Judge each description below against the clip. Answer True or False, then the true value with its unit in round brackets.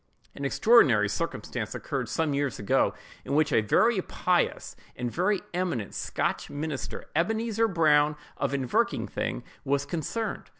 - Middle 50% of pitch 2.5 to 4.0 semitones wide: False (5.0 semitones)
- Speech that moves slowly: True (130 wpm)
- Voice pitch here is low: False (150 Hz)